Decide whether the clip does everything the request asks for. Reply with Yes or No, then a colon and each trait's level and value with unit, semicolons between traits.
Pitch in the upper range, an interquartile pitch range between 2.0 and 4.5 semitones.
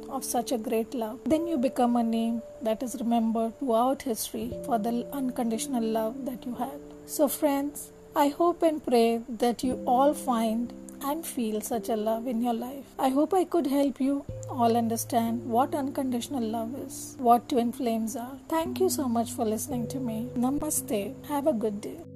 Yes: high, 245 Hz; average, 3.3 semitones